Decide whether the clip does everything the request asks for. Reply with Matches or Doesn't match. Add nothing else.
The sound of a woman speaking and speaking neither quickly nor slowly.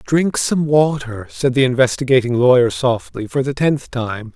Doesn't match